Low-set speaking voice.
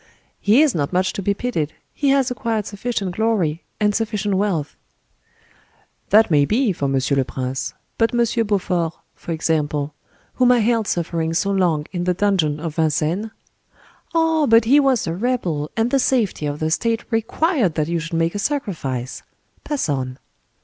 No: high, 190 Hz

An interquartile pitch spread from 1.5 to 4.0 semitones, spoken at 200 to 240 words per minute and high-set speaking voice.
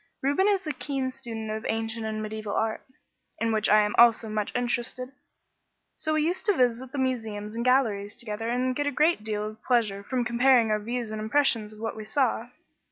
Yes: average, 3.1 semitones; fast, 205 wpm; high, 230 Hz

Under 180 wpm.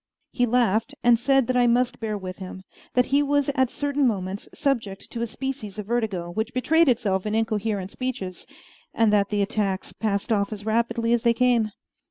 No: average, 195 wpm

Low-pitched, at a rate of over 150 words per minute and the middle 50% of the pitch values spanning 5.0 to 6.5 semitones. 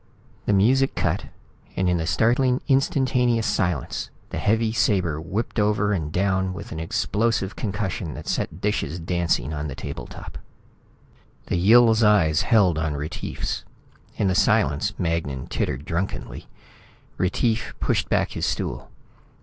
No: very low, 95 Hz; average, 140 wpm; average, 5.3 semitones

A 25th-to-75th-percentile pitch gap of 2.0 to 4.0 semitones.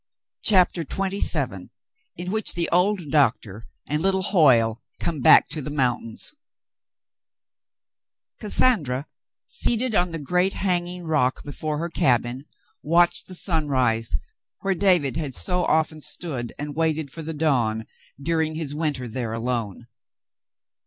No: wide, 5.5 semitones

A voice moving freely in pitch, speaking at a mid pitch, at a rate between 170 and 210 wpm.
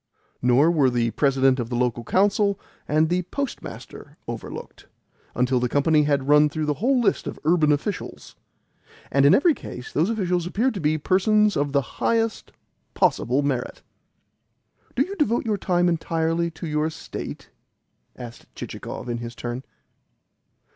No: wide, 6.0 semitones; medium, 155 Hz; average, 155 wpm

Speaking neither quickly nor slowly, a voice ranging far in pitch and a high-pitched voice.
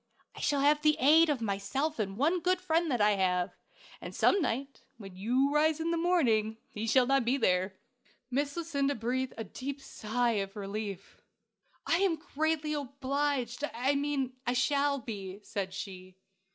Yes: average, 170 wpm; wide, 5.7 semitones; very high, 265 Hz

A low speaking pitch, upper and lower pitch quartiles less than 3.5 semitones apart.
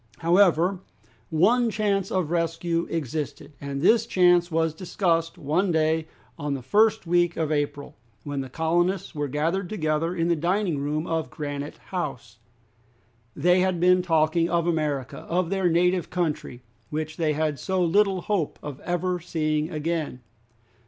No: medium, 165 Hz; average, 2.9 semitones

